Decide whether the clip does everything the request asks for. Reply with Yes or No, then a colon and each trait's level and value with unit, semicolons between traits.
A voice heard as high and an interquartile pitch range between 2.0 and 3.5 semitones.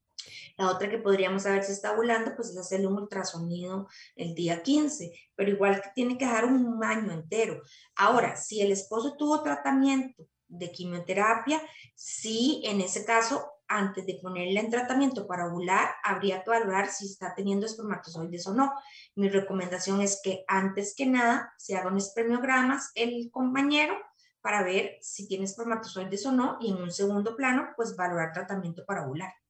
No: high, 200 Hz; average, 4.0 semitones